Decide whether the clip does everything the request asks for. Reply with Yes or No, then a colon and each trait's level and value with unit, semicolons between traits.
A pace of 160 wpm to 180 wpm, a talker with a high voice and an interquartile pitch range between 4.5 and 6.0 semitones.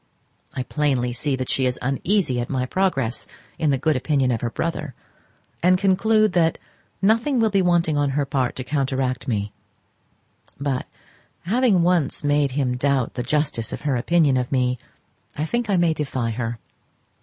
No: average, 170 wpm; medium, 140 Hz; average, 5.2 semitones